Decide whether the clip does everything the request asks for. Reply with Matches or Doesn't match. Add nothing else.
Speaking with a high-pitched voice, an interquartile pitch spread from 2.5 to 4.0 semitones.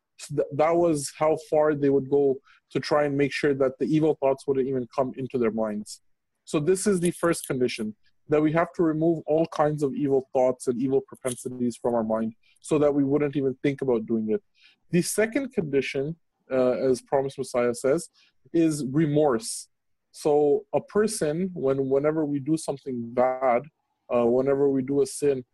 Doesn't match